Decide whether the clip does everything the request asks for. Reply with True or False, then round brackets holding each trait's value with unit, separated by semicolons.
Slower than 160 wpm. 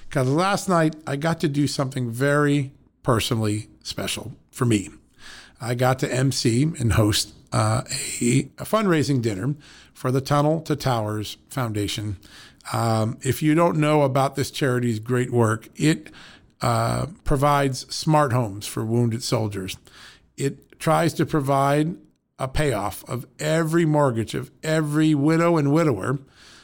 True (140 wpm)